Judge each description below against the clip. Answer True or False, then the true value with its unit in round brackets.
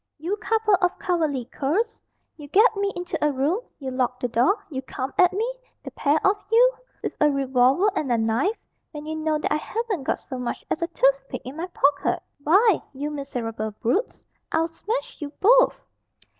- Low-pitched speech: False (305 Hz)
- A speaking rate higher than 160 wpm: True (190 wpm)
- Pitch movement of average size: False (6.9 semitones)